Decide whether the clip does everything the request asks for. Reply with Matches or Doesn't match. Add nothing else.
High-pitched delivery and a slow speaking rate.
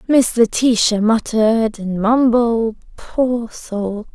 Matches